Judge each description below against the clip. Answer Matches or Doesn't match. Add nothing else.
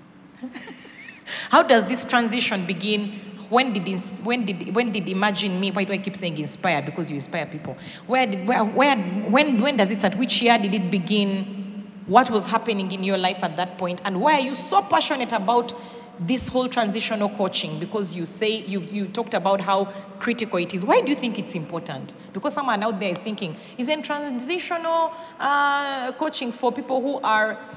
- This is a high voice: Matches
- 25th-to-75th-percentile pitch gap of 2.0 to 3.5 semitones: Doesn't match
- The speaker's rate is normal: Matches